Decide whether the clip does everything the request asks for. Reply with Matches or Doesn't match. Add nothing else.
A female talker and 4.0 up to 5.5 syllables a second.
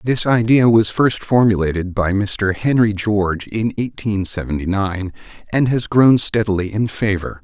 Doesn't match